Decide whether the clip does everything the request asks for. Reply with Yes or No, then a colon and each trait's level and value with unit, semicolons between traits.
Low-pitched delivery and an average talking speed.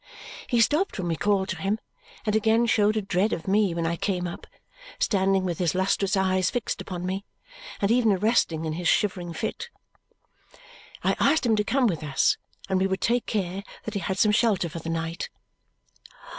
No: high, 195 Hz; average, 195 wpm